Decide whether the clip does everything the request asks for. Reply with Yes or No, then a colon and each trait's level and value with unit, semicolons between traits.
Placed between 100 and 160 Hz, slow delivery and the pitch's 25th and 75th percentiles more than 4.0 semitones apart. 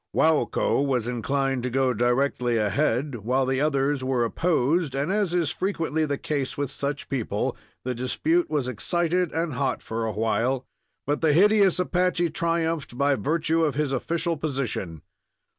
No: medium, 140 Hz; average, 155 wpm; average, 4.4 semitones